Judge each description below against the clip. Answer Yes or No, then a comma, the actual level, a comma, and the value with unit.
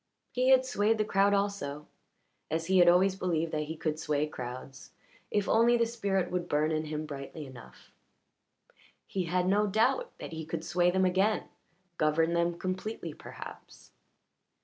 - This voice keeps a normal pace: Yes, average, 165 wpm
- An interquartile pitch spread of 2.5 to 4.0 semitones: No, average, 4.5 semitones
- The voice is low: No, medium, 180 Hz